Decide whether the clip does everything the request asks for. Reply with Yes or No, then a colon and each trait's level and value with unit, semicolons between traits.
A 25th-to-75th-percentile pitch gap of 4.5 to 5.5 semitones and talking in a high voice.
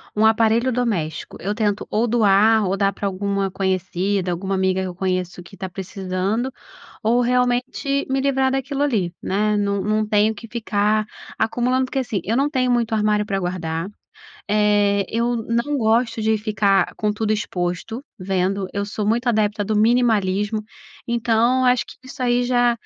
No: average, 3.5 semitones; high, 215 Hz